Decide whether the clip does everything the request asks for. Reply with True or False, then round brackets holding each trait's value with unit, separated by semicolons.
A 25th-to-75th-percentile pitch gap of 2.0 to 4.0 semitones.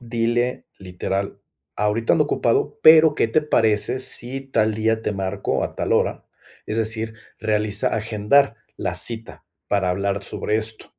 True (2.7 semitones)